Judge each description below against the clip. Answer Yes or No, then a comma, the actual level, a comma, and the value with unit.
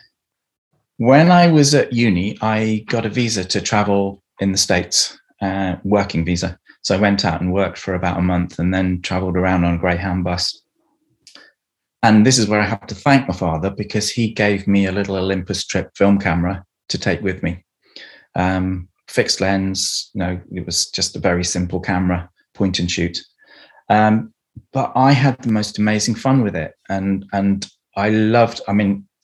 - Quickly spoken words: No, average, 185 wpm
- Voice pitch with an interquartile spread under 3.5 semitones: Yes, average, 2.7 semitones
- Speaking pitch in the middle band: No, low, 100 Hz